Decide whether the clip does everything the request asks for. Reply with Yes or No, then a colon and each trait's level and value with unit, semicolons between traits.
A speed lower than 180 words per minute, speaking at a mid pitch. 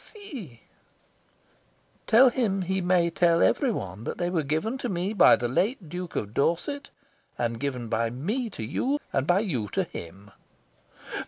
Yes: average, 160 wpm; medium, 175 Hz